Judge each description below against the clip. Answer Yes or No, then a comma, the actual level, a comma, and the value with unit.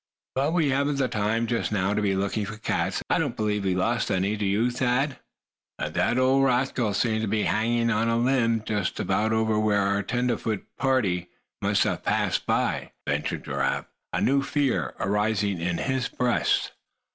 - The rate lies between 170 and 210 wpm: Yes, average, 180 wpm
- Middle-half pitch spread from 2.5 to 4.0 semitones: Yes, average, 3.5 semitones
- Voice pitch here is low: Yes, low, 110 Hz